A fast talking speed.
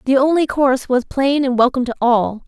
Yes: fast, 220 wpm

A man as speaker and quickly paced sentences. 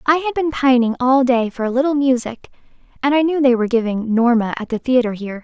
No: female; fast, 230 wpm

